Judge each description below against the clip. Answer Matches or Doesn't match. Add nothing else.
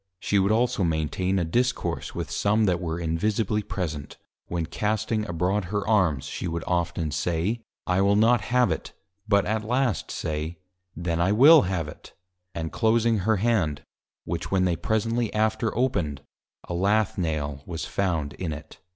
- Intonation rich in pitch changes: Doesn't match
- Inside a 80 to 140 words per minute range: Doesn't match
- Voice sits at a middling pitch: Doesn't match